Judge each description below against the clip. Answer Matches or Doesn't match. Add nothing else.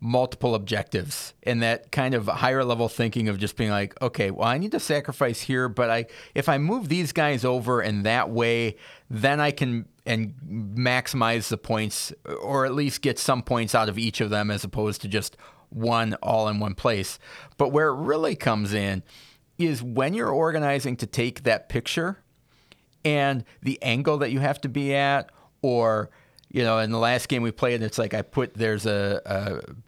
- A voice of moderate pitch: Doesn't match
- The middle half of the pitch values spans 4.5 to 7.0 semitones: Doesn't match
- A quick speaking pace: Doesn't match